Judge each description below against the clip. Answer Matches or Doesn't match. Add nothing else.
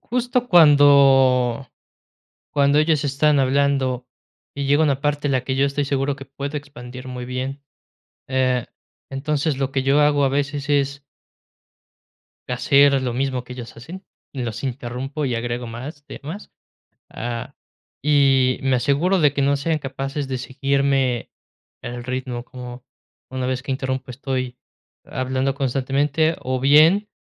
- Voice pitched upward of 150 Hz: Doesn't match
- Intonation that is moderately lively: Doesn't match